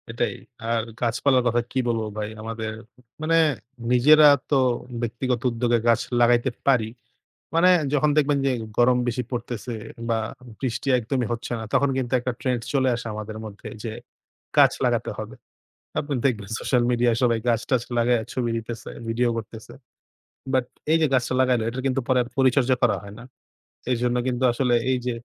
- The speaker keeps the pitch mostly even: Yes, narrow, 2.0 semitones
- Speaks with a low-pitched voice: Yes, low, 120 Hz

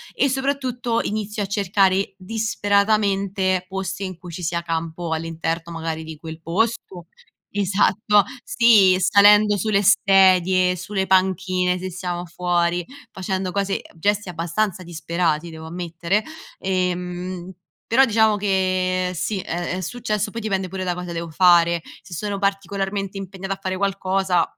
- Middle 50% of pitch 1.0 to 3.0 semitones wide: Yes, narrow, 2.5 semitones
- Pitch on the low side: No, medium, 185 Hz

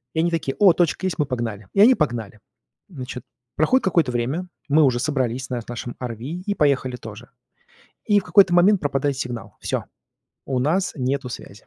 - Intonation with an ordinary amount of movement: No, wide, 5.9 semitones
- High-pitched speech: No, medium, 140 Hz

